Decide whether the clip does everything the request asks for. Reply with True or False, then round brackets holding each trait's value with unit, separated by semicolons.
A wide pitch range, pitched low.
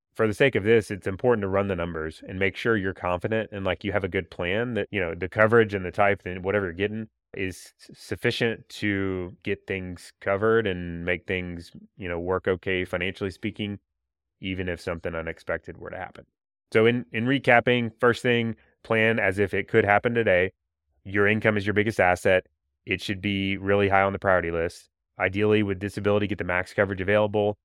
False (3.1 semitones; 100 Hz)